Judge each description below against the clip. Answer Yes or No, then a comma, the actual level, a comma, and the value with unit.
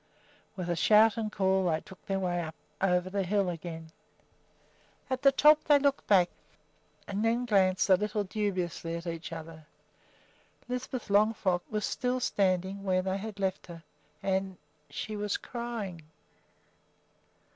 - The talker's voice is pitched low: No, high, 195 Hz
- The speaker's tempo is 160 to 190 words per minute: No, average, 145 wpm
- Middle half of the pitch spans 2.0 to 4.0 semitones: Yes, average, 3.1 semitones